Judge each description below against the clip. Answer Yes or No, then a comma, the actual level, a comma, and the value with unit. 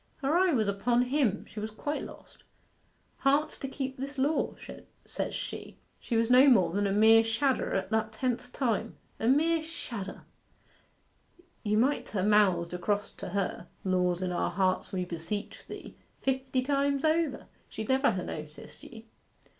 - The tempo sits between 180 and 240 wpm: No, average, 160 wpm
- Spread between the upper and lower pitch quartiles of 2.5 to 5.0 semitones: No, wide, 5.4 semitones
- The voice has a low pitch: No, high, 225 Hz